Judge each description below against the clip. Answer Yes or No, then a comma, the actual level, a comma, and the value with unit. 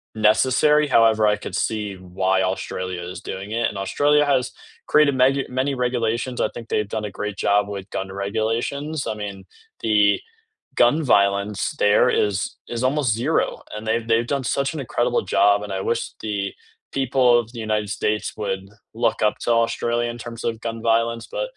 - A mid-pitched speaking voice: No, low, 115 Hz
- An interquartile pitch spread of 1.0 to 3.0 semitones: No, average, 3.4 semitones